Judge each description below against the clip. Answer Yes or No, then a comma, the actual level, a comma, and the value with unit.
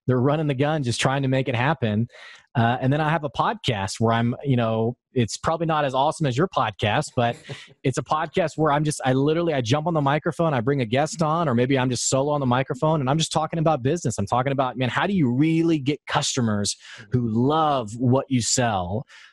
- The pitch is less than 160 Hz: Yes, medium, 140 Hz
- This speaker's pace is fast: Yes, fast, 240 wpm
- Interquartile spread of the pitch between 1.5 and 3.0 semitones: No, average, 3.9 semitones